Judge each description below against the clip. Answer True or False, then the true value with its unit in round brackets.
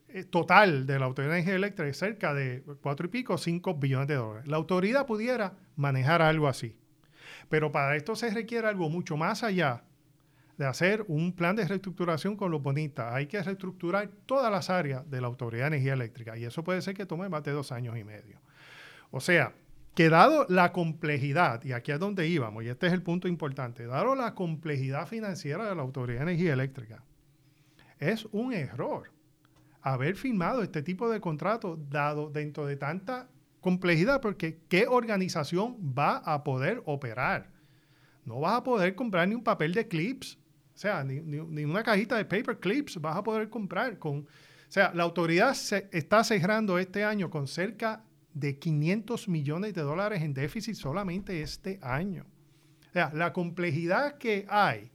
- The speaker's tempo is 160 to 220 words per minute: True (180 wpm)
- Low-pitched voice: False (165 Hz)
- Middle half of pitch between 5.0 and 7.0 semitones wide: True (5.3 semitones)